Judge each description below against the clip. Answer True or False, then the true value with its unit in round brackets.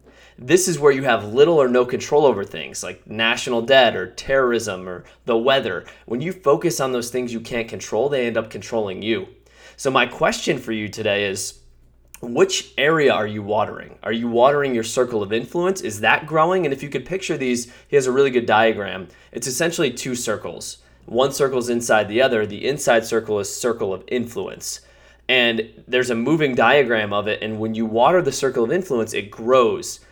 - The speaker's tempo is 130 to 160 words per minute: False (200 wpm)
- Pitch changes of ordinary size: True (4.1 semitones)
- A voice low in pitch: True (120 Hz)